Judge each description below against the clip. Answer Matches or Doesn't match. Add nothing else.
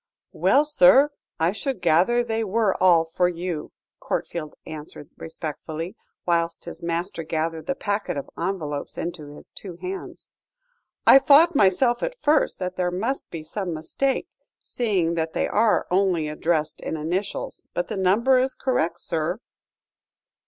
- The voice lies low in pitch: Doesn't match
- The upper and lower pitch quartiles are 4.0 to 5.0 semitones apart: Doesn't match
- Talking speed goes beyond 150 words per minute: Doesn't match